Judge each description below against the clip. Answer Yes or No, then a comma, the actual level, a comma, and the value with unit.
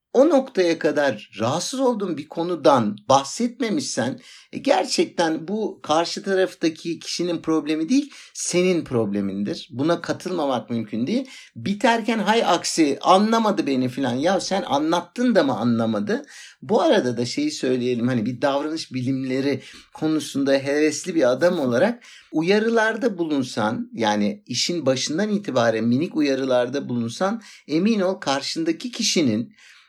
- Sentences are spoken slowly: No, average, 120 wpm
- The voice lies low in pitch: No, medium, 165 Hz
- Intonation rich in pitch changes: Yes, wide, 8.3 semitones